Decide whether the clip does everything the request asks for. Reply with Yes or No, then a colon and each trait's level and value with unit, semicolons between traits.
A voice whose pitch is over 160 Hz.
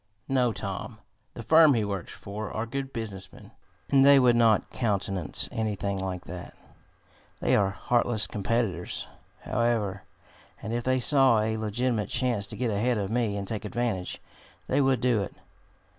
No: low, 110 Hz